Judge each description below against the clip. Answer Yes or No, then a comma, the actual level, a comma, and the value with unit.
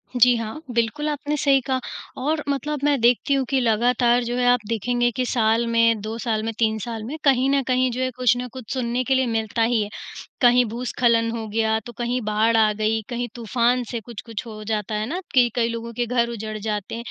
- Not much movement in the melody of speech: Yes, narrow, 2.2 semitones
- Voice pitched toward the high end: Yes, high, 235 Hz